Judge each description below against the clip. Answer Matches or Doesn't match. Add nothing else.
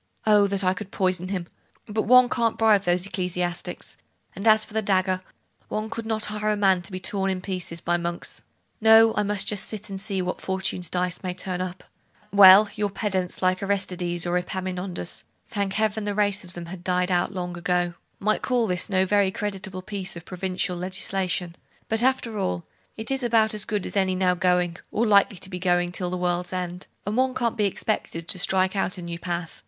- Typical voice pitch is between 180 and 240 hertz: Matches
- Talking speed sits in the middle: Doesn't match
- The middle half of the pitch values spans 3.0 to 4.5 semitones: Doesn't match